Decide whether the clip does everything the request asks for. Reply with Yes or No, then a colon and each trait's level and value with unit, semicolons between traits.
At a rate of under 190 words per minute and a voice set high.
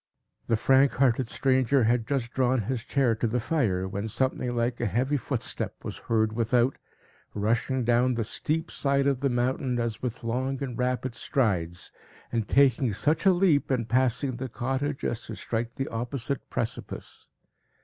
No: average, 170 wpm; low, 125 Hz